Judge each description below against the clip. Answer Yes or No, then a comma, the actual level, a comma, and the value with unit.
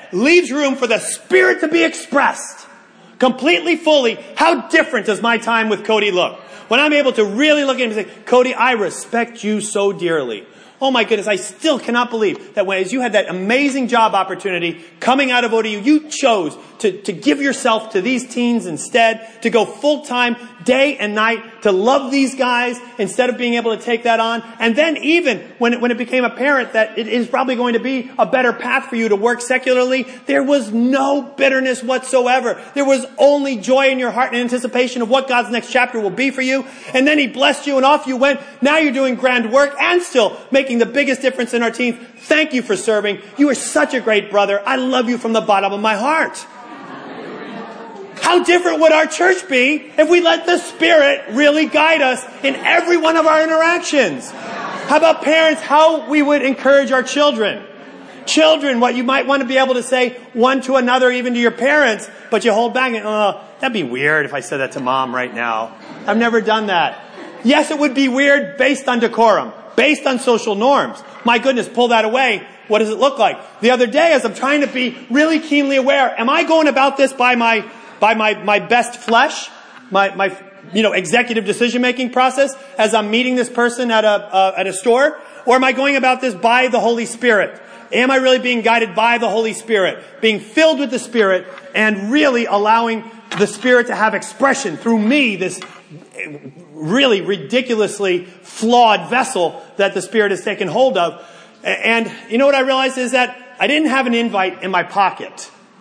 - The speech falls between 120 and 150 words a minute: No, fast, 205 wpm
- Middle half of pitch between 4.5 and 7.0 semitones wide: No, average, 3.7 semitones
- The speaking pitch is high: Yes, very high, 250 Hz